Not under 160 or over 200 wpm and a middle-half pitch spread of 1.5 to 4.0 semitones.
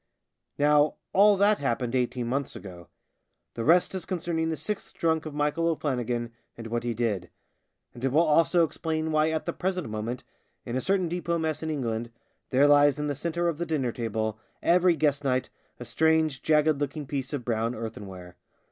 No: average, 185 wpm; average, 5.2 semitones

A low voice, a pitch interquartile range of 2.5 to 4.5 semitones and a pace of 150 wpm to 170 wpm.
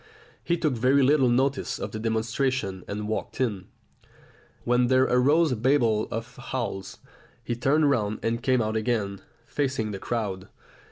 Yes: low, 120 Hz; average, 3.4 semitones; average, 155 wpm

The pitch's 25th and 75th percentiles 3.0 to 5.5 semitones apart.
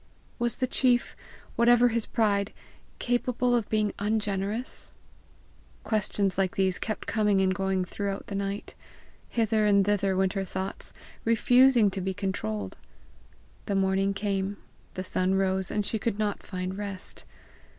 No: narrow, 2.4 semitones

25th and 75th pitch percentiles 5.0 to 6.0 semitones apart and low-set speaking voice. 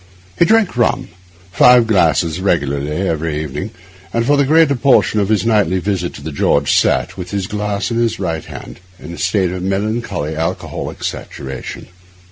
Yes: wide, 5.5 semitones; very low, 95 Hz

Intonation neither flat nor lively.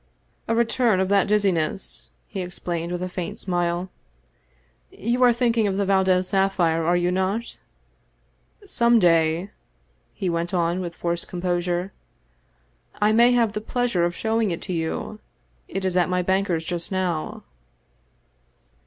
Yes: average, 3.0 semitones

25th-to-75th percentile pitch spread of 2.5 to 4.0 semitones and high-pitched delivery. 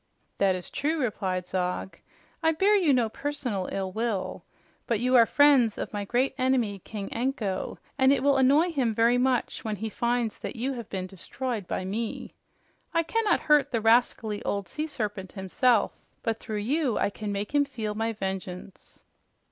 No: average, 4.8 semitones; high, 230 Hz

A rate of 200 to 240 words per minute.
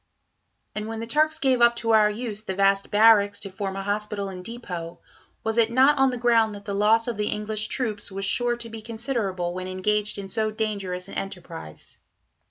Yes: fast, 205 wpm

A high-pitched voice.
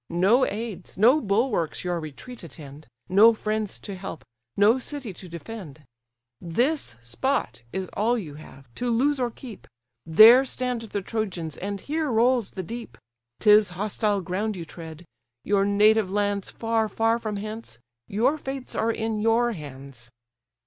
Yes: high, 210 Hz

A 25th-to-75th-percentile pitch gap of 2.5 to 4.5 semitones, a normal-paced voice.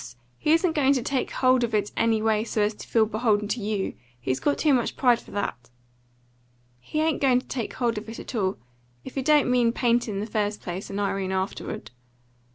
No: average, 3.7 semitones; fast, 220 wpm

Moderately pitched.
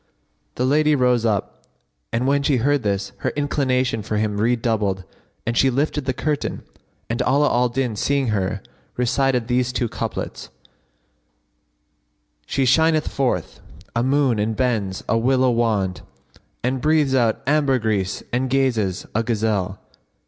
No: low, 125 Hz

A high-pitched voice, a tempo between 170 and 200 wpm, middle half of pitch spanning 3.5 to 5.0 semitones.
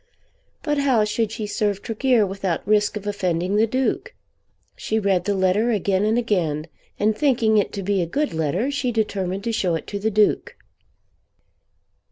No: high, 210 Hz; average, 175 wpm; average, 3.0 semitones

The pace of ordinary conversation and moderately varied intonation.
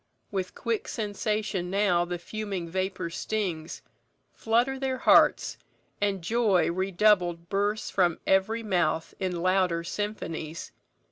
No: slow, 115 wpm; average, 3.5 semitones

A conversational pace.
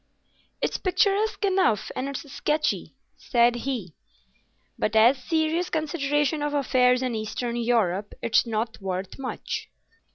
No: slow, 130 wpm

